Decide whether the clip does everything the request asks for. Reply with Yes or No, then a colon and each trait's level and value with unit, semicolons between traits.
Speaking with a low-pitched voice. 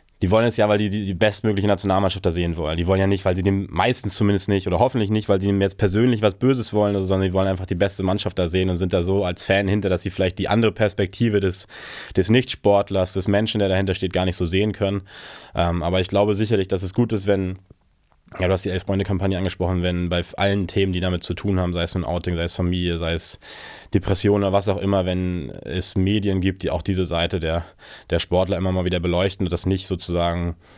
Yes: very low, 95 Hz